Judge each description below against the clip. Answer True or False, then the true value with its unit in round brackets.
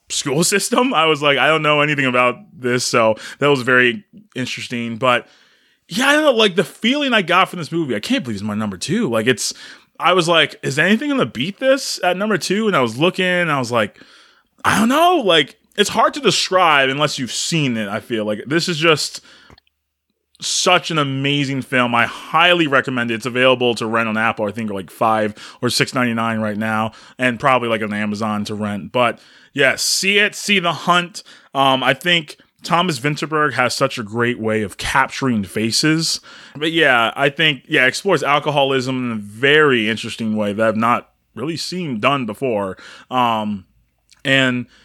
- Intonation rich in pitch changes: True (7.3 semitones)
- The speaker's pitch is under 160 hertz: True (135 Hz)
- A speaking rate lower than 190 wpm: False (200 wpm)